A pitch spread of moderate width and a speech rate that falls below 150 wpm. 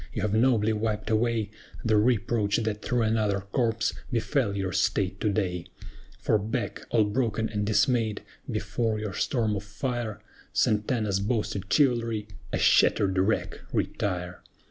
No: narrow, 2.2 semitones; average, 140 wpm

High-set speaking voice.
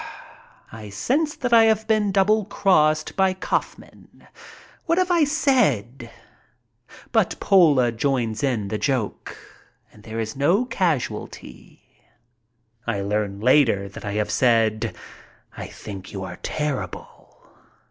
No: low, 135 Hz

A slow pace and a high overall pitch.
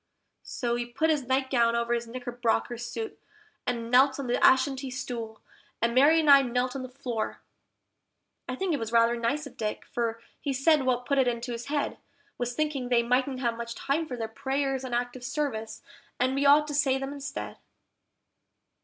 No: average, 190 wpm; very high, 255 Hz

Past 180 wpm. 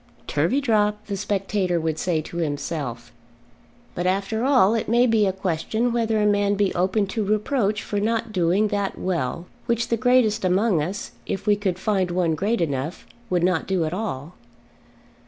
No: average, 175 wpm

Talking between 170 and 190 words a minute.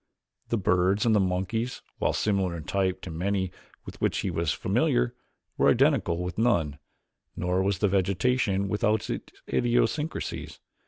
No: average, 150 wpm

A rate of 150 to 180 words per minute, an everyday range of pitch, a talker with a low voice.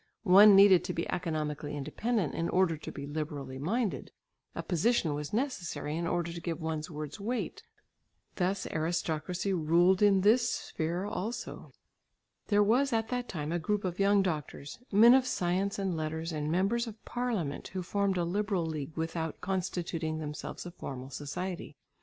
No: average, 165 wpm; average, 4.3 semitones; medium, 175 Hz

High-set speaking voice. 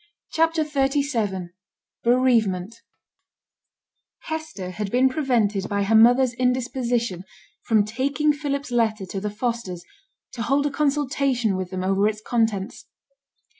Yes: high, 235 Hz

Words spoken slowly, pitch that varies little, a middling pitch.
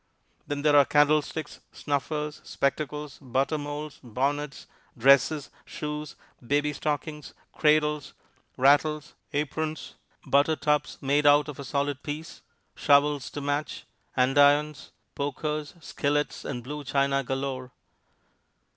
Yes: slow, 110 wpm; narrow, 1.4 semitones; medium, 145 Hz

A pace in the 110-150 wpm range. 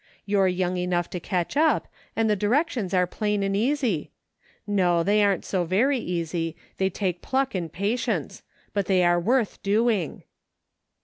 No: average, 160 wpm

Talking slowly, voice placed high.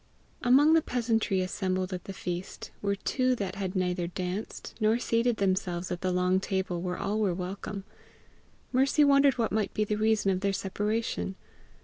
No: average, 170 wpm; high, 200 Hz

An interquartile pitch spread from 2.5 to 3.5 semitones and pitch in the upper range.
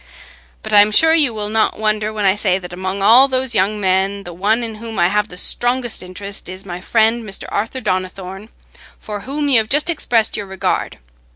Yes: average, 3.2 semitones; high, 210 Hz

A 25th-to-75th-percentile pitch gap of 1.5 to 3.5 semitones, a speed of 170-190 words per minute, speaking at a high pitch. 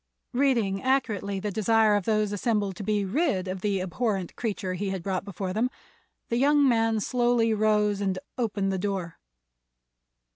No: average, 2.9 semitones; average, 160 wpm; high, 210 Hz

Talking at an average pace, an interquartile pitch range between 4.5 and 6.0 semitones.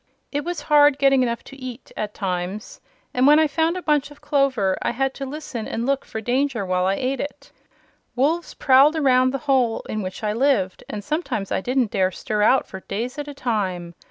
No: fast, 215 wpm; average, 5.2 semitones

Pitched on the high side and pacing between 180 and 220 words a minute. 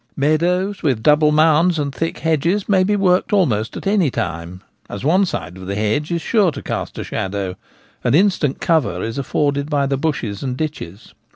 No: medium, 150 Hz; average, 190 wpm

